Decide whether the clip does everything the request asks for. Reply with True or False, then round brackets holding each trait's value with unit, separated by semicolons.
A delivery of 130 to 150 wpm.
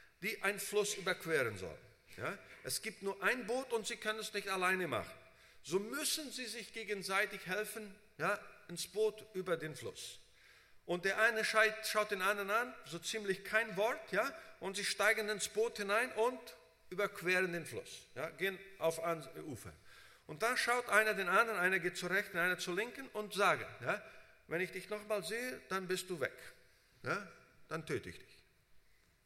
False (180 wpm)